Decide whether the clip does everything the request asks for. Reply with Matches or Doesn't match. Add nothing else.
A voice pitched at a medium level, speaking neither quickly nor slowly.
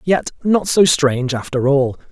Matches